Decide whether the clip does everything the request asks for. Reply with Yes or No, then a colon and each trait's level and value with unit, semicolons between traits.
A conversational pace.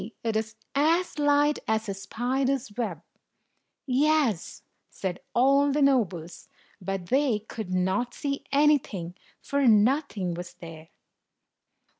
No: slow, 115 wpm